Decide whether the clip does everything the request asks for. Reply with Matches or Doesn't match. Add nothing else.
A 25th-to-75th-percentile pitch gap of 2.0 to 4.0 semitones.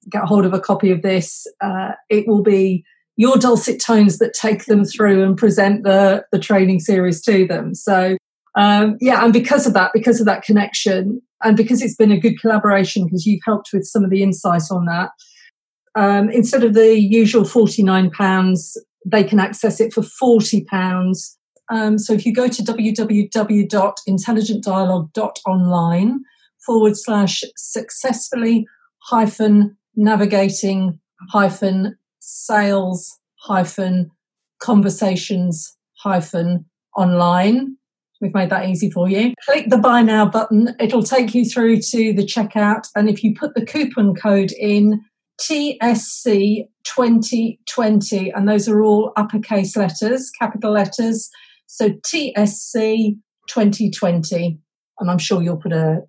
Matches